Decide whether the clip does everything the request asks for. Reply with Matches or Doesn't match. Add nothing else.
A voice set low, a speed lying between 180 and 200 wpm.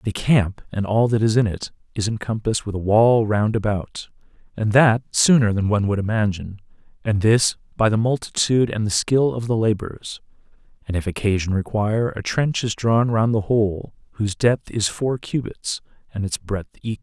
Matches